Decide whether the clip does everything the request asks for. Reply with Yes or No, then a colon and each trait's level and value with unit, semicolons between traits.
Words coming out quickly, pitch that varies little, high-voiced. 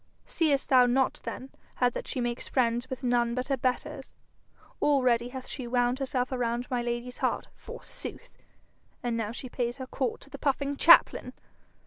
No: average, 170 wpm; narrow, 1.7 semitones; very high, 250 Hz